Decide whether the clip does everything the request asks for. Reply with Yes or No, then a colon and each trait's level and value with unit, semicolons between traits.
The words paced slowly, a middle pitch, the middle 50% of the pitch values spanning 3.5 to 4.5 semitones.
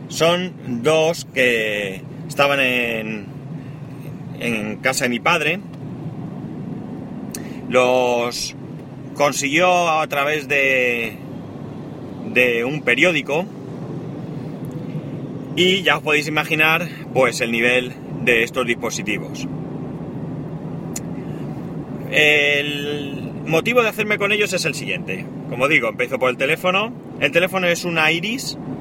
Yes: slow, 100 wpm; medium, 145 Hz; average, 3.8 semitones